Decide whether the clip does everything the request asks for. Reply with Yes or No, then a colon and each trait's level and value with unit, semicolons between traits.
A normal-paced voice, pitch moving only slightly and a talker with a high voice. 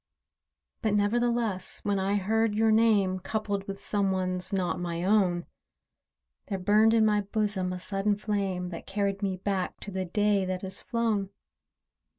Yes: average, 160 wpm; narrow, 2.2 semitones; high, 200 Hz